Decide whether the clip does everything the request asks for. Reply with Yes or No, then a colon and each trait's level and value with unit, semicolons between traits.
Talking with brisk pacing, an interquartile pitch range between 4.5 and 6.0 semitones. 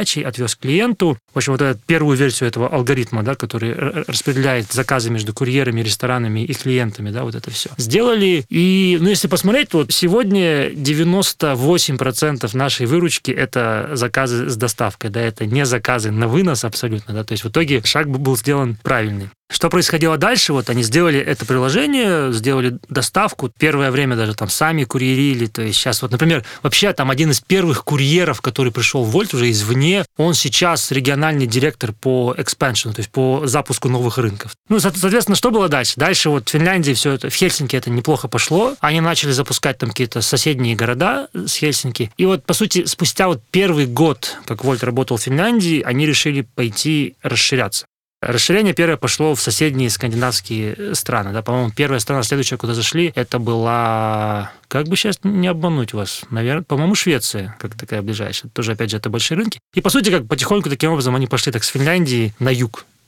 Yes: fast, 180 wpm; average, 5.0 semitones